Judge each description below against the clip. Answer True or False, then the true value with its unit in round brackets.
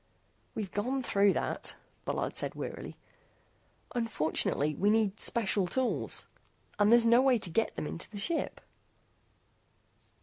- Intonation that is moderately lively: True (3.2 semitones)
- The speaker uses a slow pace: True (130 wpm)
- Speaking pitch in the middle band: False (215 Hz)